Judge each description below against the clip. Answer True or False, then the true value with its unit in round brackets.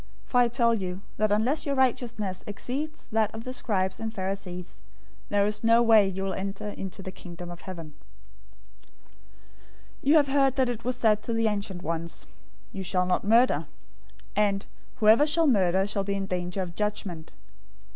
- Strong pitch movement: False (3.8 semitones)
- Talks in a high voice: True (205 Hz)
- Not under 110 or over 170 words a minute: False (185 wpm)